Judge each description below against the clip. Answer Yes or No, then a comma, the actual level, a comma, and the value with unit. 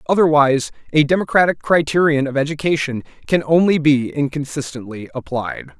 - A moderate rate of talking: No, slow, 115 wpm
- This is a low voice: No, medium, 150 Hz